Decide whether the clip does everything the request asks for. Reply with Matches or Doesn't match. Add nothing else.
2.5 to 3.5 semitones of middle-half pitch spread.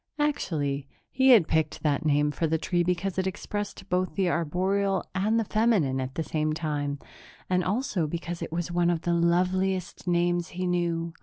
Matches